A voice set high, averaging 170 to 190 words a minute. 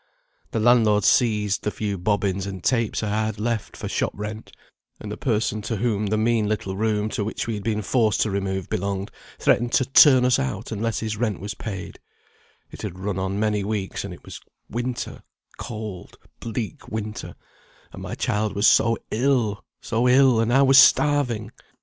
No: low, 110 Hz; average, 185 wpm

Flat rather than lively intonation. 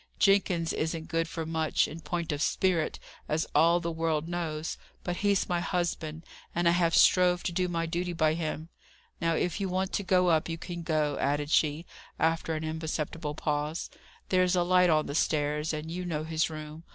Yes: narrow, 2.1 semitones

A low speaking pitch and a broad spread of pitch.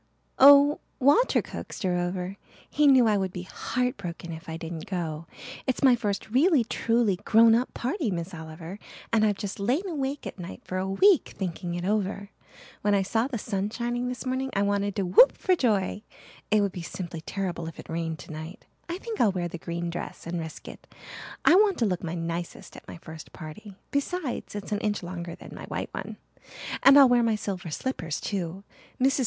No: high, 200 Hz; wide, 6.1 semitones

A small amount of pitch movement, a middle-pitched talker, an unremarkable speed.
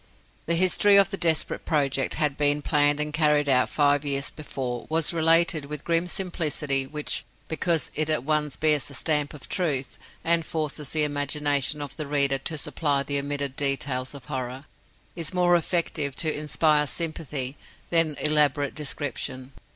Yes: narrow, 2.2 semitones; medium, 150 Hz; average, 165 wpm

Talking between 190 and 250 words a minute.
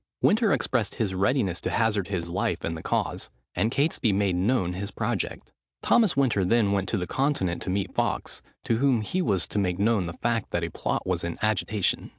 Yes: fast, 205 wpm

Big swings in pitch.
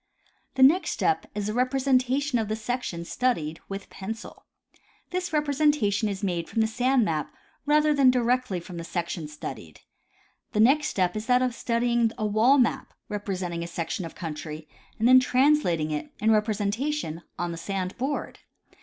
Yes: wide, 6.3 semitones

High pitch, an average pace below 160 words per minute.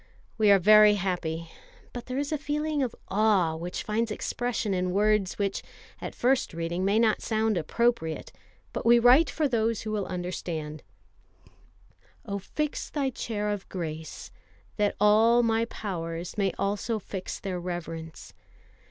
Yes: high, 210 Hz; average, 150 wpm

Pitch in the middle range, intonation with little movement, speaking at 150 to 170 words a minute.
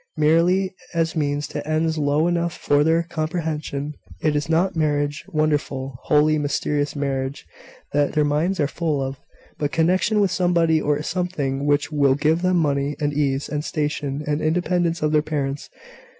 Yes: medium, 150 Hz; narrow, 2.3 semitones; average, 165 wpm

